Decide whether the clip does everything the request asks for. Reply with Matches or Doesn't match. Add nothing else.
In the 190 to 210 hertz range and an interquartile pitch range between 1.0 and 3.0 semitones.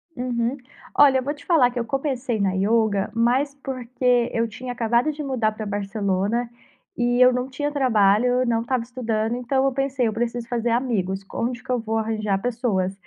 Doesn't match